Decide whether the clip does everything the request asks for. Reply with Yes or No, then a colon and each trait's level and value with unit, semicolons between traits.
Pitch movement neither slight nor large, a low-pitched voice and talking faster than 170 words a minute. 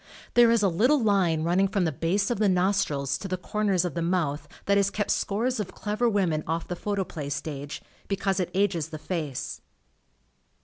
No: average, 3.8 semitones; medium, 185 Hz; average, 190 wpm